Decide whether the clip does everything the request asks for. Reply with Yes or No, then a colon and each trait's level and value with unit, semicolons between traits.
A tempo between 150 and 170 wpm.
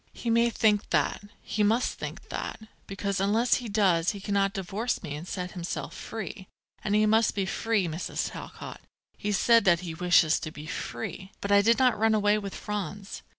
No: average, 195 wpm